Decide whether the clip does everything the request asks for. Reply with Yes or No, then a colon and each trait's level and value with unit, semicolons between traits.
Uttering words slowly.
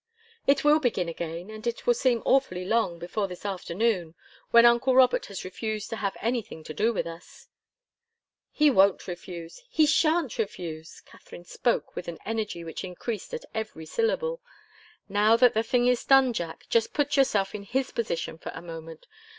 No: average, 175 wpm